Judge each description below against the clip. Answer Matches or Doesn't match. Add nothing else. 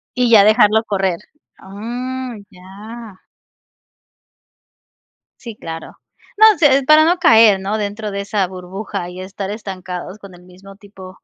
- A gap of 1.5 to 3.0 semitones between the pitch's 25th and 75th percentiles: Doesn't match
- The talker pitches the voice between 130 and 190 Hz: Doesn't match